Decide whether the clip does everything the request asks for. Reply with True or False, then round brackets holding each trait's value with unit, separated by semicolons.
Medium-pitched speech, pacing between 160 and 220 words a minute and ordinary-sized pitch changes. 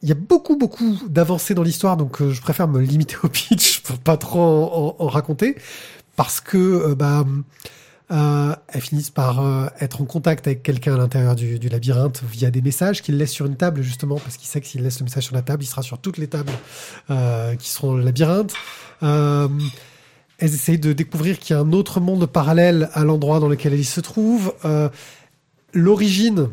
True (150 Hz; 215 wpm; 3.7 semitones)